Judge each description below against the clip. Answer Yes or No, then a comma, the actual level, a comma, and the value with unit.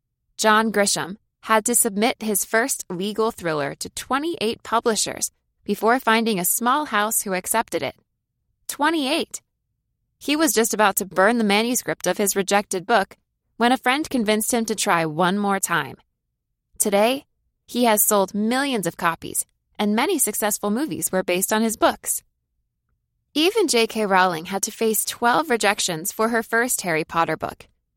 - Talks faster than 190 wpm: No, average, 155 wpm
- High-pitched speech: Yes, high, 215 Hz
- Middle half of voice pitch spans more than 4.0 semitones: No, average, 3.6 semitones